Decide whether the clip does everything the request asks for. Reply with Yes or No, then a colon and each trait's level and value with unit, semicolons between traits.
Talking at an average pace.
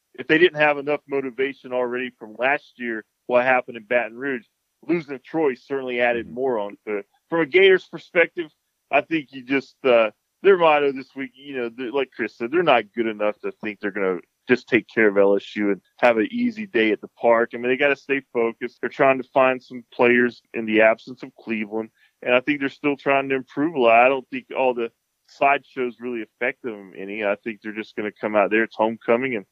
No: fast, 230 wpm